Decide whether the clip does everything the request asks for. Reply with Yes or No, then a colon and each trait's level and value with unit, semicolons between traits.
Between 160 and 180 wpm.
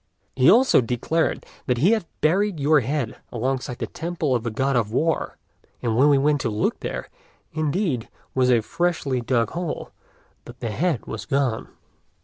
Yes: average, 170 wpm